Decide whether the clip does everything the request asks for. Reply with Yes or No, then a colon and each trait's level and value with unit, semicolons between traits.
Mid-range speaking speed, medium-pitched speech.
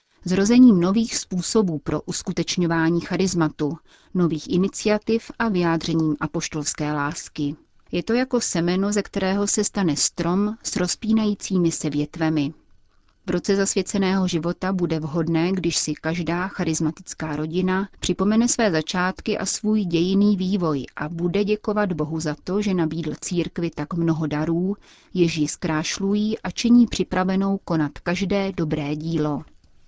Yes: average, 130 wpm; medium, 175 Hz